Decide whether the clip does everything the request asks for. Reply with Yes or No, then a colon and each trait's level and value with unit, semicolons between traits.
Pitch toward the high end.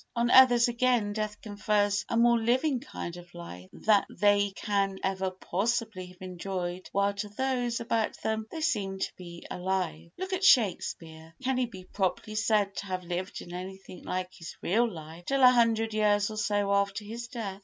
Yes: high, 205 Hz